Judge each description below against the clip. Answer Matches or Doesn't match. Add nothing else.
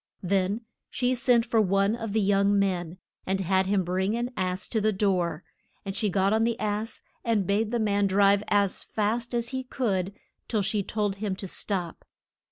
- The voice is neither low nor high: Doesn't match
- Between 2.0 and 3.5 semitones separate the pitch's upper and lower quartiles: Matches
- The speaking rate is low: Doesn't match